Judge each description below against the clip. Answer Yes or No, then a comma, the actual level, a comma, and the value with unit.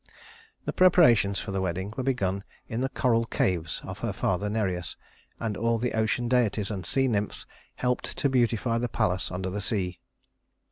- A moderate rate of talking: Yes, average, 175 wpm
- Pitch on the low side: Yes, low, 110 Hz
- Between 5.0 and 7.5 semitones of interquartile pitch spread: No, average, 4.2 semitones